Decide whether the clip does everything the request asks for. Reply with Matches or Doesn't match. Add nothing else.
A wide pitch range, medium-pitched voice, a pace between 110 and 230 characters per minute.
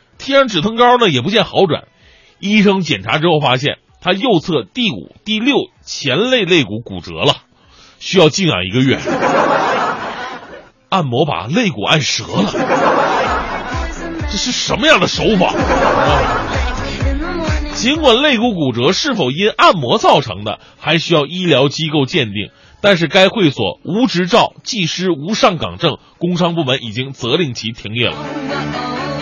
Matches